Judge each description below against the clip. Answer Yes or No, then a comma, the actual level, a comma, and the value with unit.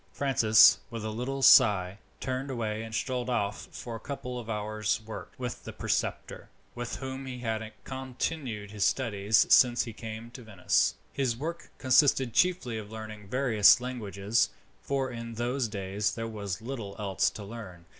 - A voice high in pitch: No, low, 115 Hz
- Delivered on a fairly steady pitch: No, average, 3.2 semitones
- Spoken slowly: No, average, 165 wpm